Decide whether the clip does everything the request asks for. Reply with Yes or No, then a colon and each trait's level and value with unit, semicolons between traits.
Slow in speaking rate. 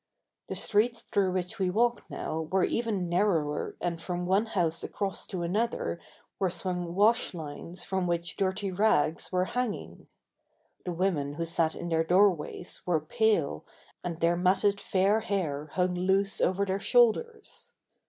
No: average, 155 wpm